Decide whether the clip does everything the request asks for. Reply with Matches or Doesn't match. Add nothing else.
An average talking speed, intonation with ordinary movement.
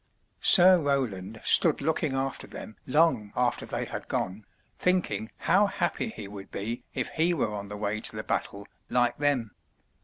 Doesn't match